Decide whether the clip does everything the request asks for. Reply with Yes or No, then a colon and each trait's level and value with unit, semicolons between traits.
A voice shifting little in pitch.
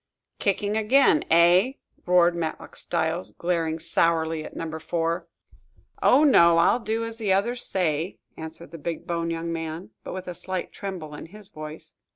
No: average, 3.3 semitones